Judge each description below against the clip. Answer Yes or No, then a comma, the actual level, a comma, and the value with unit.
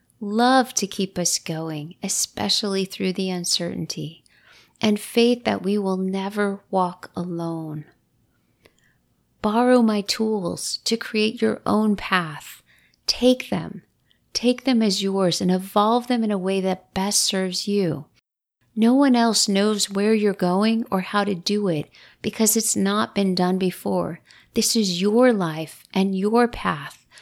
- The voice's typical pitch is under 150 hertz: No, high, 200 Hz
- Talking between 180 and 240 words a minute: No, average, 145 wpm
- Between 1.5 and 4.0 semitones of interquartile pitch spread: Yes, average, 3.0 semitones